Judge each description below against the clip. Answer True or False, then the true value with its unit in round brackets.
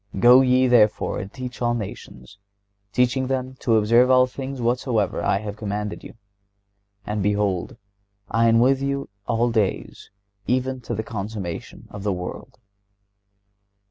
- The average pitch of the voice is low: True (115 Hz)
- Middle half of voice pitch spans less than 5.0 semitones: True (3.6 semitones)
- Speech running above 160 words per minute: False (140 wpm)